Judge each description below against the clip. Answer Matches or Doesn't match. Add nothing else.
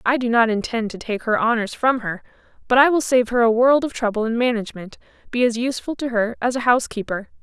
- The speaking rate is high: Matches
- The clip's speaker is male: Doesn't match